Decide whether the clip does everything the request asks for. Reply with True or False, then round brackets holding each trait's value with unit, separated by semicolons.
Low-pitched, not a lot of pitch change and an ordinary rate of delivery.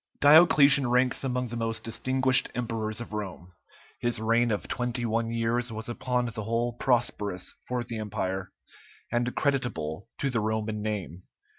True (115 Hz; 2.3 semitones; 150 wpm)